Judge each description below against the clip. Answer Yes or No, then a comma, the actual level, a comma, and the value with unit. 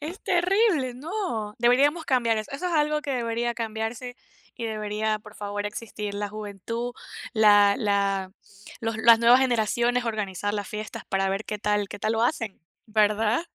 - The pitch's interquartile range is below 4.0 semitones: Yes, average, 3.0 semitones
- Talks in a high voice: Yes, high, 225 Hz